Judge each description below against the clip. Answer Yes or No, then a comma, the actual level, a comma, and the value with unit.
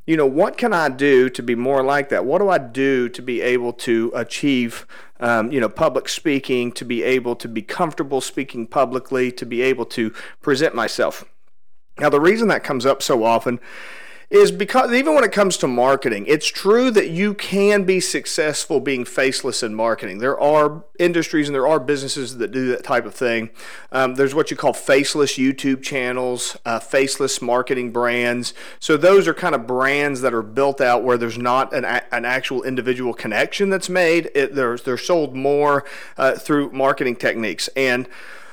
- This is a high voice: No, low, 135 Hz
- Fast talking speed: No, average, 190 wpm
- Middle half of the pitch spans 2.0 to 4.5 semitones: Yes, average, 4.0 semitones